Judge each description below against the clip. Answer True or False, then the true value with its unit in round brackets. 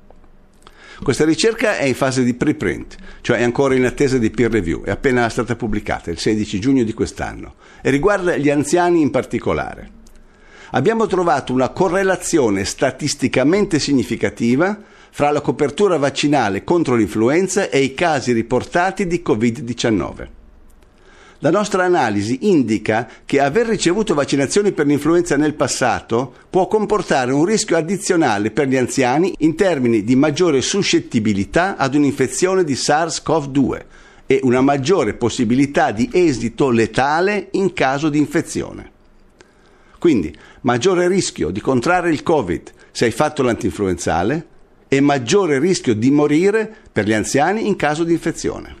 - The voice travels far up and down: True (6.7 semitones)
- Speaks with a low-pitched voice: False (145 Hz)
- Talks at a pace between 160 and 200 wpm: False (135 wpm)